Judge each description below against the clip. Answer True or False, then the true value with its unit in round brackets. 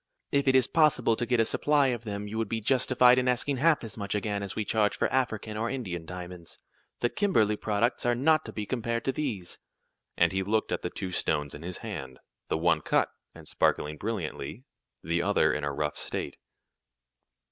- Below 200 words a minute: False (205 wpm)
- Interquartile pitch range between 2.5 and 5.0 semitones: False (5.6 semitones)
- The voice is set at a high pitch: False (110 Hz)